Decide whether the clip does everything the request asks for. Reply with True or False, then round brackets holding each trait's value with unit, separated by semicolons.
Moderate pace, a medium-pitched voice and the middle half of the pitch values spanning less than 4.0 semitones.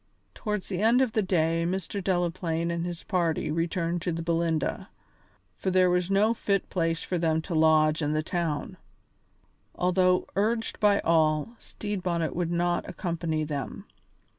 True (160 wpm; 175 Hz; 2.4 semitones)